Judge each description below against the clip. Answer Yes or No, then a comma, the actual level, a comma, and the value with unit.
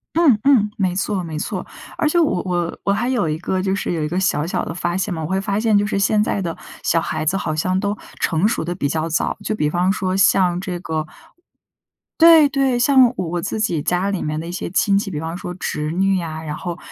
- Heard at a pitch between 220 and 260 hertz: No, medium, 185 Hz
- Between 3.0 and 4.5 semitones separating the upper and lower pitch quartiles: Yes, average, 3.7 semitones